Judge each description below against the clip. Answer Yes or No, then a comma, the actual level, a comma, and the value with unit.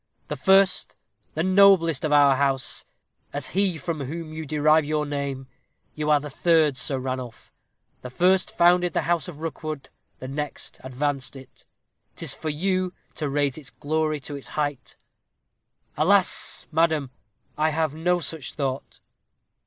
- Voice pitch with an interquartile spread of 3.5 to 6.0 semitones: No, average, 3.0 semitones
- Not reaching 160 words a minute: Yes, average, 150 wpm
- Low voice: No, medium, 150 Hz